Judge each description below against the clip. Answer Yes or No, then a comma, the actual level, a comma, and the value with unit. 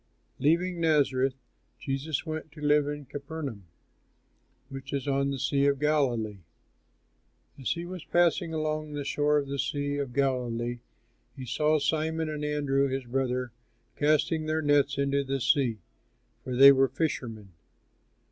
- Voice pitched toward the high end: No, medium, 140 Hz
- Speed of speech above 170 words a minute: No, average, 145 wpm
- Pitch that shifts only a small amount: Yes, narrow, 2.3 semitones